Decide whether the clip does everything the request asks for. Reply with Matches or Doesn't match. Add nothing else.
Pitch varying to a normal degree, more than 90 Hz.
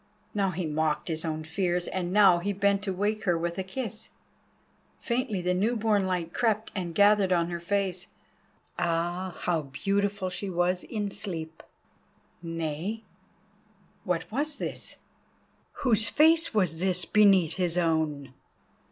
Matches